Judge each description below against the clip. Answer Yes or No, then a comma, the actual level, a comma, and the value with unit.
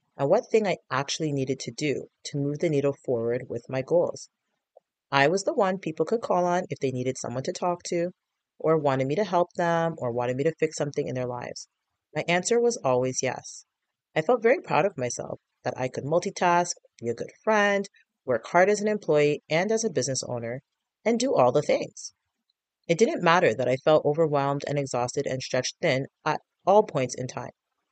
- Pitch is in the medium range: Yes, medium, 150 Hz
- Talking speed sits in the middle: No, fast, 210 wpm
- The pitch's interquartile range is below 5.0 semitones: No, wide, 5.4 semitones